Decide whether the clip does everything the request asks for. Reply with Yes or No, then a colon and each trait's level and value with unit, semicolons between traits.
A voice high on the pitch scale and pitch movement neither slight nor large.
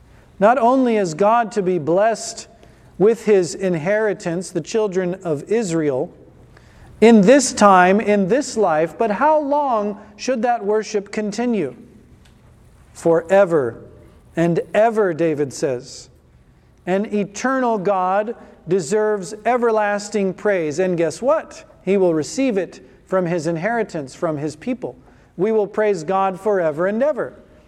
Yes: high, 205 Hz; average, 4.0 semitones